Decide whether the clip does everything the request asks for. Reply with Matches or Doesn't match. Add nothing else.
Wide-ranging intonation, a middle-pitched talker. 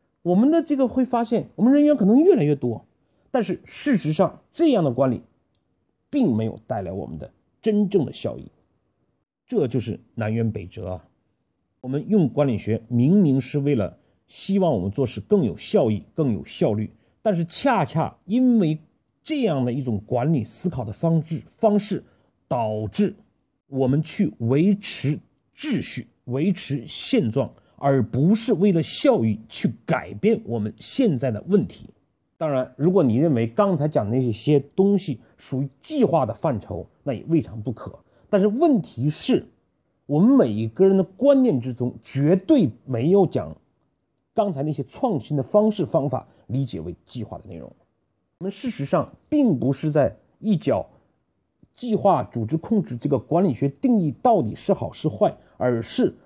Matches